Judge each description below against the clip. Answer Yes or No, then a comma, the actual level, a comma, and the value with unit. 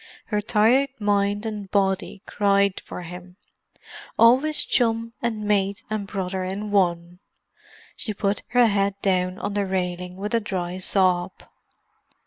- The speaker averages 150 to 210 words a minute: No, slow, 135 wpm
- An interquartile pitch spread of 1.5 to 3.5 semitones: Yes, narrow, 2.4 semitones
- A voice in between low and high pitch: No, high, 200 Hz